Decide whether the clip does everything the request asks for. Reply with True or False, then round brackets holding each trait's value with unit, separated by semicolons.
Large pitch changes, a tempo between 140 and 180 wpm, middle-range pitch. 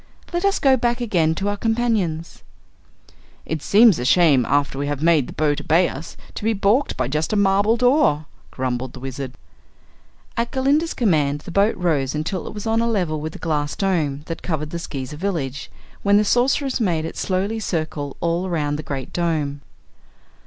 False (6.2 semitones; 190 wpm; 170 Hz)